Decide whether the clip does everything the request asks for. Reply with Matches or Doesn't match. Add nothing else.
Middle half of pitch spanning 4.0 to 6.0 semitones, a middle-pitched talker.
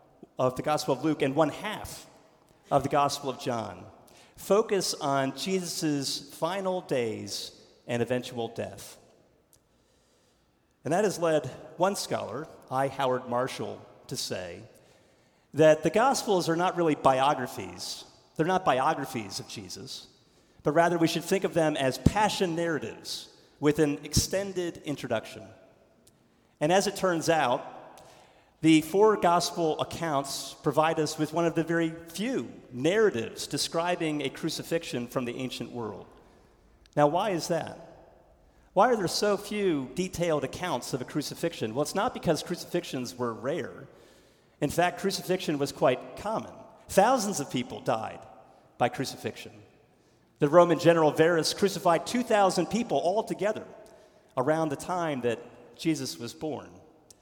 Matches